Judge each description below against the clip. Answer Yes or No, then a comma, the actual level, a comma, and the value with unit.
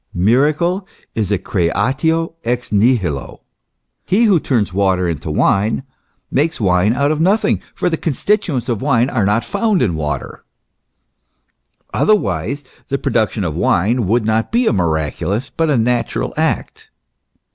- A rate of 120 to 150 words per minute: Yes, average, 140 wpm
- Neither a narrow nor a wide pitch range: No, wide, 7.8 semitones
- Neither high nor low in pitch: No, low, 120 Hz